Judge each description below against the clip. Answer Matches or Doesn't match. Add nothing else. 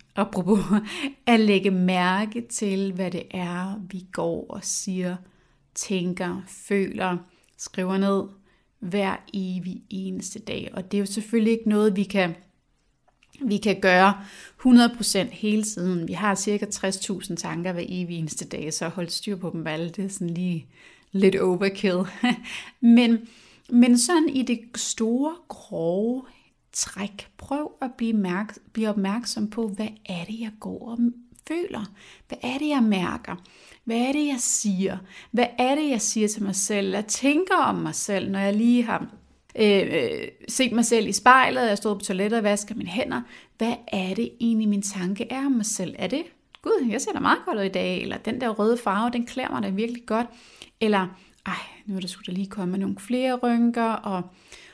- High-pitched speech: Matches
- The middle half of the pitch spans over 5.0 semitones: Doesn't match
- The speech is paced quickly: Doesn't match